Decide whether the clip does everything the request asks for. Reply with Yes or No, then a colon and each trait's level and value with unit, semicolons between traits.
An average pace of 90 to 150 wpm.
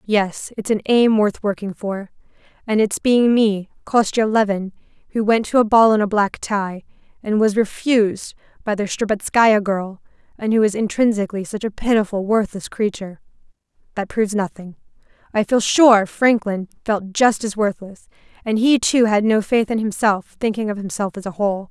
No: average, 170 wpm